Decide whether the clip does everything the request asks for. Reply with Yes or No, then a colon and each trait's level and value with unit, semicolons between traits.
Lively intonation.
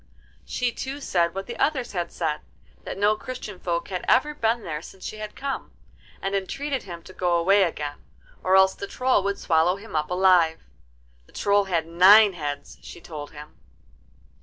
No: average, 4.0 semitones